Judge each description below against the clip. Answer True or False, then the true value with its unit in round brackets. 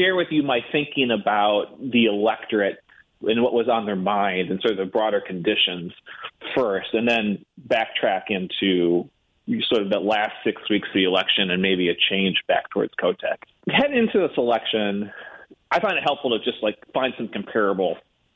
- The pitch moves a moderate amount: True (3.9 semitones)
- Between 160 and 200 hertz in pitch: False (105 Hz)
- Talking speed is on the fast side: False (180 wpm)